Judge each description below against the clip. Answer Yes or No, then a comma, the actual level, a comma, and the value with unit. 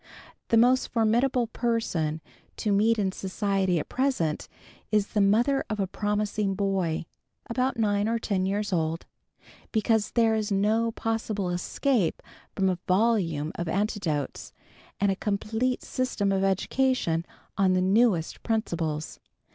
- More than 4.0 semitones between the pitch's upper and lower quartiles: No, average, 3.4 semitones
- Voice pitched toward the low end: No, high, 205 Hz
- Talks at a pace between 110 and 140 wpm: Yes, slow, 135 wpm